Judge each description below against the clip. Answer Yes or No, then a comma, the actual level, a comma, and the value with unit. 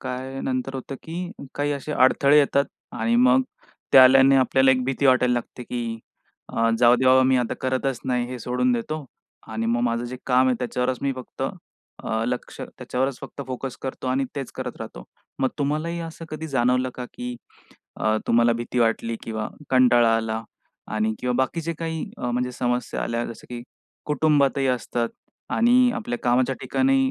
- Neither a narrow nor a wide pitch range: No, narrow, 2.1 semitones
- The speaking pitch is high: No, low, 130 Hz